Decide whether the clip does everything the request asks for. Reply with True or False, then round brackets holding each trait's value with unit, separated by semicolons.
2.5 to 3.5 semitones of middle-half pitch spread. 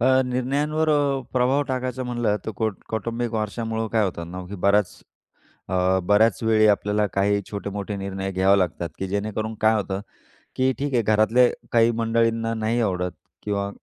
True (3.0 semitones)